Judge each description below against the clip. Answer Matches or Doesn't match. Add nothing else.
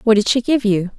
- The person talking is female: Matches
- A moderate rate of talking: Doesn't match